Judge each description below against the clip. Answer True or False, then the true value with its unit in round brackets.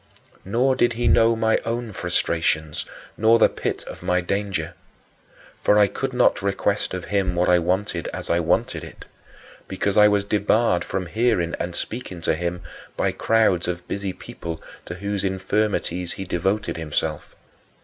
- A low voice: True (95 Hz)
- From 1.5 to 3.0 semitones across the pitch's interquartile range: False (3.5 semitones)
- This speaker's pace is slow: False (160 wpm)